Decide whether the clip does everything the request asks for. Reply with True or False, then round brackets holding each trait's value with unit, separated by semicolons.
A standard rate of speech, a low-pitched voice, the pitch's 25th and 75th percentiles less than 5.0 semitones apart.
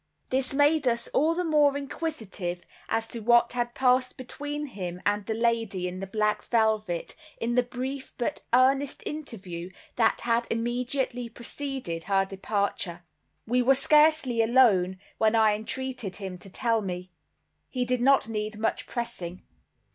False (150 wpm; 235 Hz; 4.3 semitones)